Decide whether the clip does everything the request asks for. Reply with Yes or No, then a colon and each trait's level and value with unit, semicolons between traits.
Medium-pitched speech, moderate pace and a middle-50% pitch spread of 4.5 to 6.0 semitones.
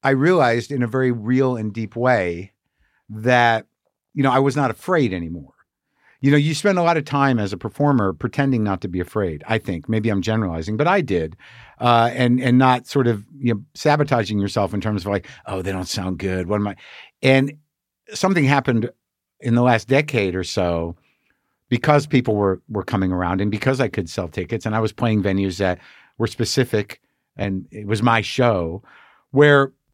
No: low, 115 Hz; average, 195 wpm; average, 5.0 semitones